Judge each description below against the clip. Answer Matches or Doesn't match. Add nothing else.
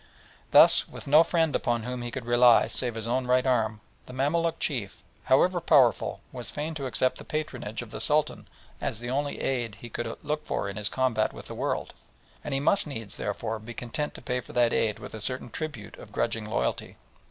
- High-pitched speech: Doesn't match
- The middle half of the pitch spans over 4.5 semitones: Doesn't match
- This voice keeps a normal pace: Doesn't match